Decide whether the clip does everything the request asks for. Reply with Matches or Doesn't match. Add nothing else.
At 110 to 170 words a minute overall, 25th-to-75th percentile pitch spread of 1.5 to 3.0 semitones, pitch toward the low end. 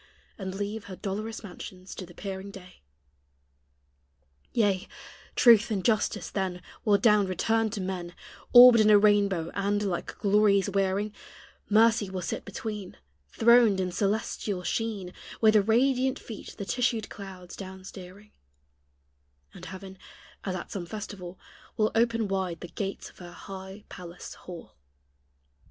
Doesn't match